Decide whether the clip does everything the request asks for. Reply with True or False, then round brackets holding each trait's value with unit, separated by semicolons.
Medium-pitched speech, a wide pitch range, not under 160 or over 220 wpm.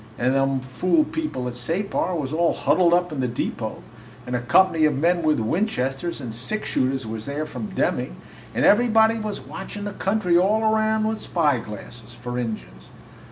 True (155 Hz; 8.1 semitones; 175 wpm)